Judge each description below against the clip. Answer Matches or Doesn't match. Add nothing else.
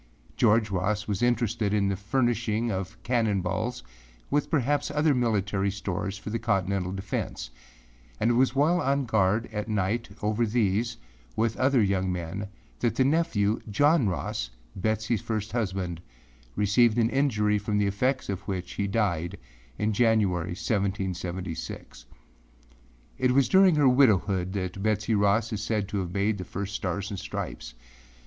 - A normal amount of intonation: Matches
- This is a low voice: Matches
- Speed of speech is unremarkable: Matches